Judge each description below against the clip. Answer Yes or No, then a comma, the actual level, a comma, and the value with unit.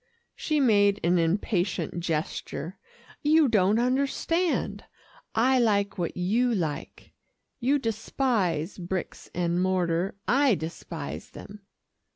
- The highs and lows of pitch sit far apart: Yes, wide, 6.0 semitones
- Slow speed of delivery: Yes, slow, 105 wpm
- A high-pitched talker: Yes, high, 200 Hz